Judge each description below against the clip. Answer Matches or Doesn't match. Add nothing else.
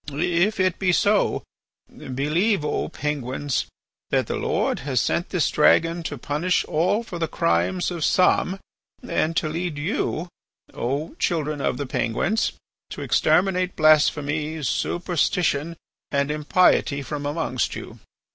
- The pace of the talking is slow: Matches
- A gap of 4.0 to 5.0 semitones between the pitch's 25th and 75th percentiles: Doesn't match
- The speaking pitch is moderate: Matches